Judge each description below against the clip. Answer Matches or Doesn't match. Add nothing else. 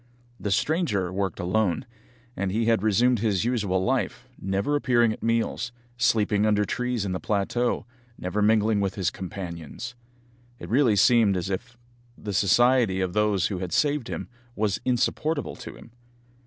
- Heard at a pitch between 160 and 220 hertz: Doesn't match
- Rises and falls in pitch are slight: Doesn't match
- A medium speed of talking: Matches